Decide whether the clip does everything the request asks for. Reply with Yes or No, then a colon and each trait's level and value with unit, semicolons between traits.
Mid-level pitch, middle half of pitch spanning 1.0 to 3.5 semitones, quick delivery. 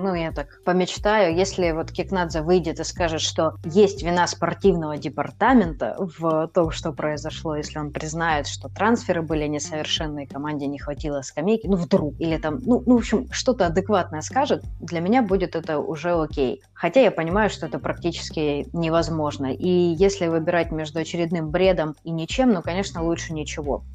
Yes: medium, 165 Hz; average, 3.0 semitones; fast, 165 wpm